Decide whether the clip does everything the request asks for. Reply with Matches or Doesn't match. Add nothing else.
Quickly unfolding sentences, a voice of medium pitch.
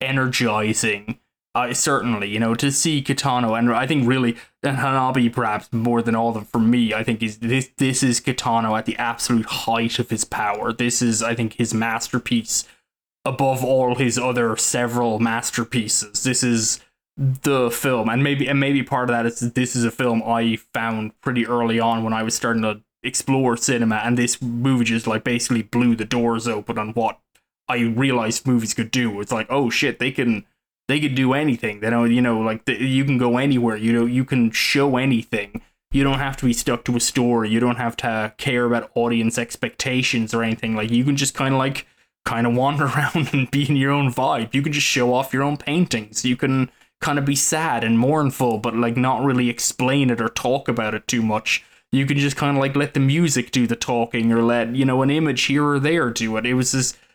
Doesn't match